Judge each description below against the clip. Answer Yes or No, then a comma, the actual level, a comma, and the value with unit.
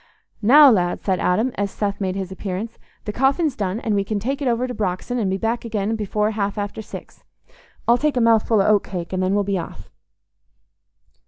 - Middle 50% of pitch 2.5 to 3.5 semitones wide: Yes, average, 3.2 semitones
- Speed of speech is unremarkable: No, fast, 215 wpm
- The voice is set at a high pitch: Yes, high, 210 Hz